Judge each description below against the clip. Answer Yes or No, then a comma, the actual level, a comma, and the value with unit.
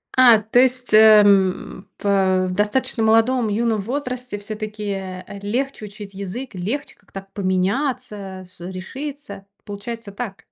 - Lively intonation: No, average, 3.9 semitones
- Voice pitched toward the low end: No, high, 210 Hz